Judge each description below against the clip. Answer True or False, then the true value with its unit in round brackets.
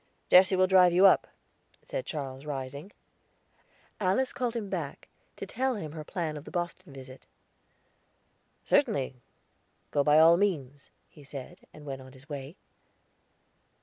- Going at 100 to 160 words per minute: True (145 wpm)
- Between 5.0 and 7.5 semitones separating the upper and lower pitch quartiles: True (5.3 semitones)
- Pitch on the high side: False (155 Hz)